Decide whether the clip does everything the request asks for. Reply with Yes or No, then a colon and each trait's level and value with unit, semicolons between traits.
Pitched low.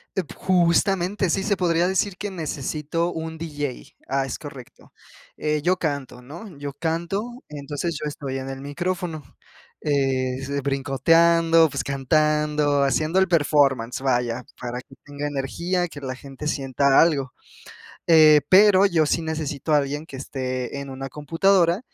No: medium, 150 Hz